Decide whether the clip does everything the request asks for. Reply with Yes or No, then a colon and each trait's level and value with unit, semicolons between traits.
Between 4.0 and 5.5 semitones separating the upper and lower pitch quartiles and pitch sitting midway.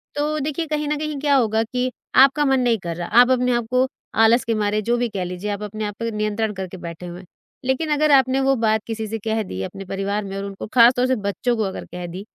No: average, 4.5 semitones; high, 225 Hz